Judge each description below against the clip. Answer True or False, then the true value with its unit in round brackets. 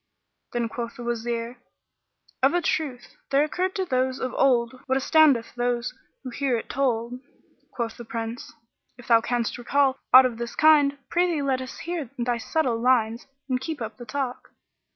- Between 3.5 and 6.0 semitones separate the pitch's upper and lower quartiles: False (2.8 semitones)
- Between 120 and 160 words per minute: False (175 wpm)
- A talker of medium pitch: False (255 Hz)